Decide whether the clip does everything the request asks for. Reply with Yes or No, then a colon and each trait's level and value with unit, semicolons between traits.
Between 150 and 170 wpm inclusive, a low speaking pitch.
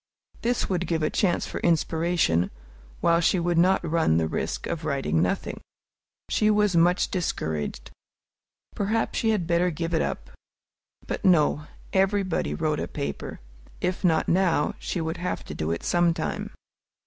No: average, 155 wpm; medium, 170 Hz